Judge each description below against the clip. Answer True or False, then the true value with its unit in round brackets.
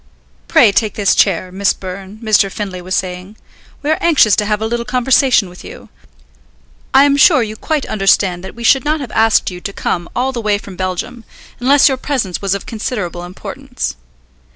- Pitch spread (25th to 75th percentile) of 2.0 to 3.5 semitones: False (5.0 semitones)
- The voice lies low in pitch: False (215 Hz)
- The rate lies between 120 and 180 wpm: False (195 wpm)